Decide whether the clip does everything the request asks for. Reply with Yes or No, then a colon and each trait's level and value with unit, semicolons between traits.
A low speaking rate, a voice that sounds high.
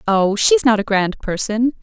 No: average, 200 wpm; high, 220 Hz